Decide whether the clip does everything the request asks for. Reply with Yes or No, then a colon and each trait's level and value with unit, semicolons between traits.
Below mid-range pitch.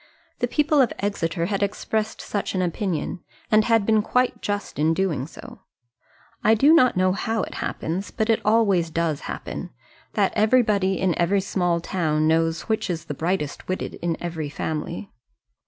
No: high, 190 Hz